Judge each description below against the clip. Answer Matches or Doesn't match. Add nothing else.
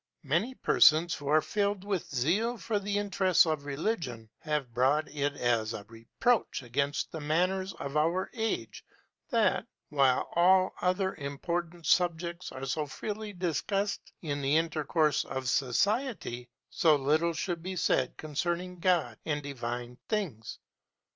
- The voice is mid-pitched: Matches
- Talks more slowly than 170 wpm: Matches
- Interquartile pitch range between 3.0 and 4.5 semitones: Doesn't match